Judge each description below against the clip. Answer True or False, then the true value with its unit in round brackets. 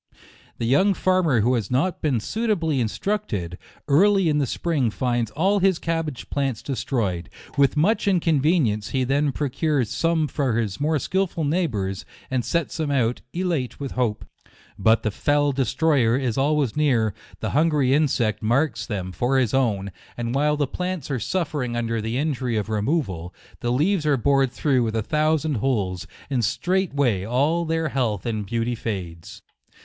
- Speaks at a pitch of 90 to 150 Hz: True (135 Hz)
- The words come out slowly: False (170 wpm)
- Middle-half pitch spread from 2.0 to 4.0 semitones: False (5.5 semitones)